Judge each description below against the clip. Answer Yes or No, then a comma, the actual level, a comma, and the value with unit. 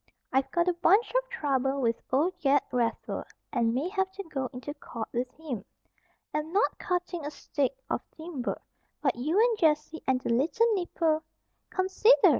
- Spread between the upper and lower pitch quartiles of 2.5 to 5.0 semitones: No, wide, 5.6 semitones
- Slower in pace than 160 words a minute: No, average, 170 wpm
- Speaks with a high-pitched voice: Yes, very high, 305 Hz